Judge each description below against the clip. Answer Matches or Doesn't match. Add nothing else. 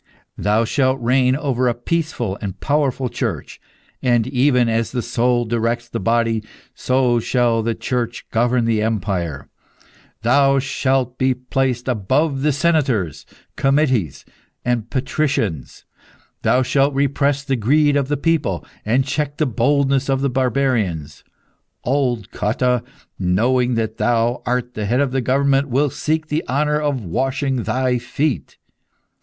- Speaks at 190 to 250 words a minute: Doesn't match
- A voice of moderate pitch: Doesn't match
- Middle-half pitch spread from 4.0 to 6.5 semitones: Doesn't match